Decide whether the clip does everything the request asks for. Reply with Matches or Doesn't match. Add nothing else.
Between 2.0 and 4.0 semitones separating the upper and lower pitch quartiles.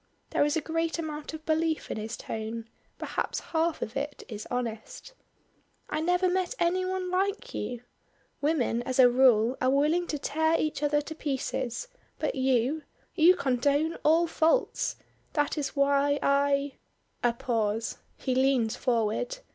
Doesn't match